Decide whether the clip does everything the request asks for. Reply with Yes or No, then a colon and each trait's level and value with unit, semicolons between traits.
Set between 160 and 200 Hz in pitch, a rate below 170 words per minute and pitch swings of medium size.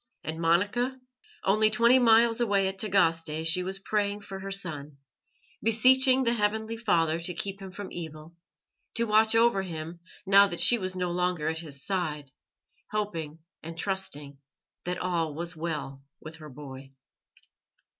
Yes: medium, 185 Hz; average, 155 wpm; average, 4.7 semitones